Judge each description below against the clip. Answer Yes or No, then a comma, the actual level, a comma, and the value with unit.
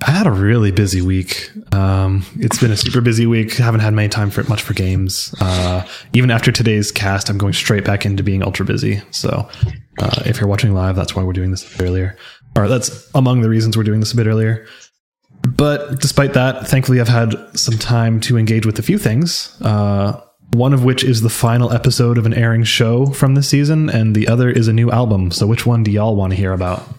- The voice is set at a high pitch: No, low, 110 Hz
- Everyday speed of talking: No, fast, 240 wpm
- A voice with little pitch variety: No, average, 3.6 semitones